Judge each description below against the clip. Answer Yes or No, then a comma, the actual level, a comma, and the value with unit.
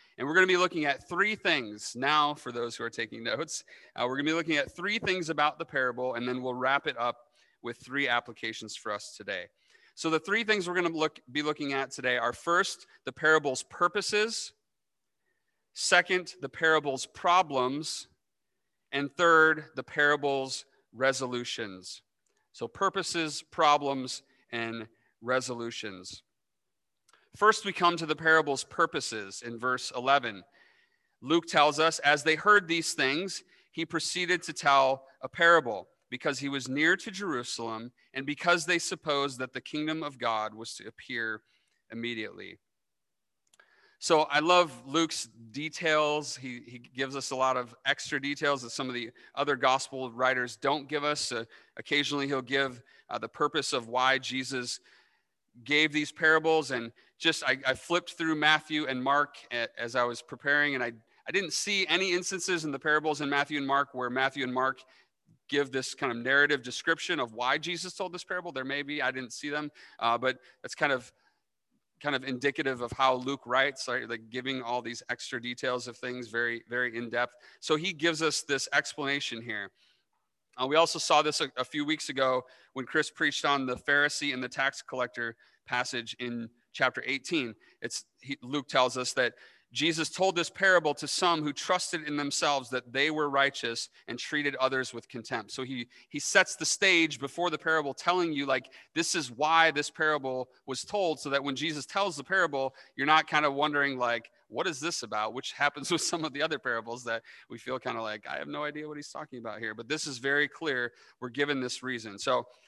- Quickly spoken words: No, average, 185 wpm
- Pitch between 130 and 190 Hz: Yes, medium, 140 Hz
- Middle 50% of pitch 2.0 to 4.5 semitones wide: Yes, average, 3.9 semitones